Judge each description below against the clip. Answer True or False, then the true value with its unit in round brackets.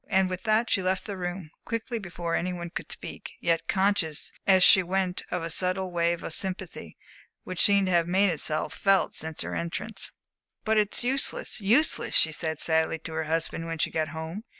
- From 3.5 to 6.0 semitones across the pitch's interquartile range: False (2.8 semitones)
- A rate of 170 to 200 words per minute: True (195 wpm)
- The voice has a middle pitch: True (180 Hz)